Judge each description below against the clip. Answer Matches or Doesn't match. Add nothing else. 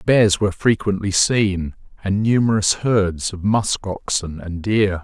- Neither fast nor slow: Matches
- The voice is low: Matches